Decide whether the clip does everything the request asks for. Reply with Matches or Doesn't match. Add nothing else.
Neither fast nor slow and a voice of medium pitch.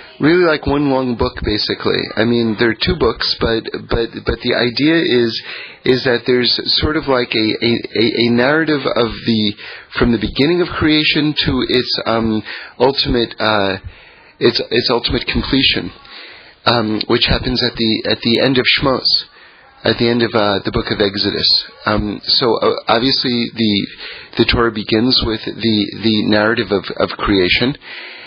Doesn't match